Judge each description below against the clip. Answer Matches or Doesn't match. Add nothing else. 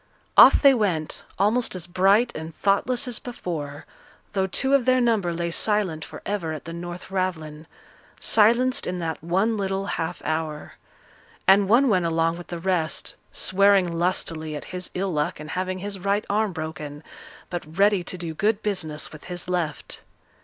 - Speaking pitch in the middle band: Matches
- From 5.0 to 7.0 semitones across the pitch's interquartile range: Doesn't match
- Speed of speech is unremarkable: Matches